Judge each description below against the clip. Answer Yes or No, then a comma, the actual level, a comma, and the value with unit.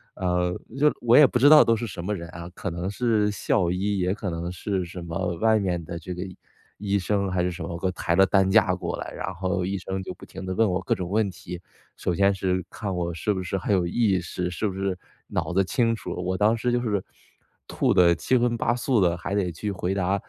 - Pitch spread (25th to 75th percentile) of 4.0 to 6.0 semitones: No, average, 2.7 semitones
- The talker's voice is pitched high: No, very low, 95 Hz